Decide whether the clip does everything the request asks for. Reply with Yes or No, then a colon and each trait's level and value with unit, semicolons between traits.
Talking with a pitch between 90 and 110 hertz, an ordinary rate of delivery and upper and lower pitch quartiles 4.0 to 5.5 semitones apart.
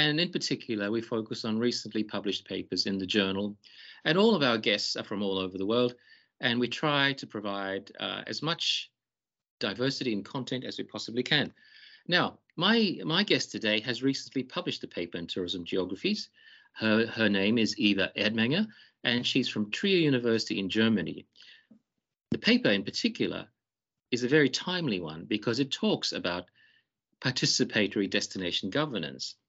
No: low, 120 Hz; average, 165 wpm; average, 5.0 semitones